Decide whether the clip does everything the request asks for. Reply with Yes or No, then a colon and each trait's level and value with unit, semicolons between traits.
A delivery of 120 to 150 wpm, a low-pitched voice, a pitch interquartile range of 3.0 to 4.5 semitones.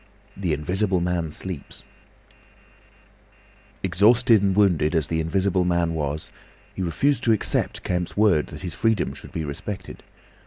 Yes: average, 140 wpm; very low, 90 Hz; average, 3.7 semitones